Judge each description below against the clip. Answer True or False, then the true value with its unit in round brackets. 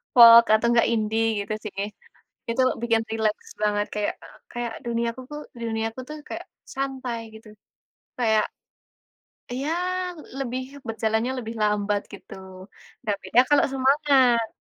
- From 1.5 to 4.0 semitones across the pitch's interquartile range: True (2.6 semitones)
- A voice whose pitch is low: False (230 Hz)